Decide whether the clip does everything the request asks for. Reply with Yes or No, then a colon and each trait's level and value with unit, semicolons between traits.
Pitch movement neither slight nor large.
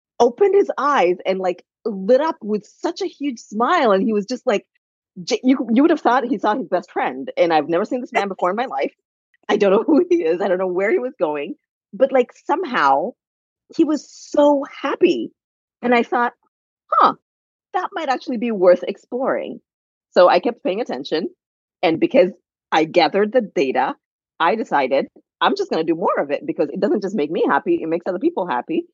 No: wide, 8.3 semitones